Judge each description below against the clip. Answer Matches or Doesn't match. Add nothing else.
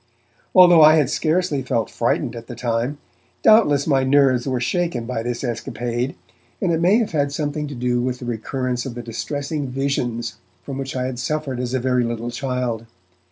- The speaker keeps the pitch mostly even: Doesn't match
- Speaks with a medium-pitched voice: Doesn't match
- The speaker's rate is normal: Matches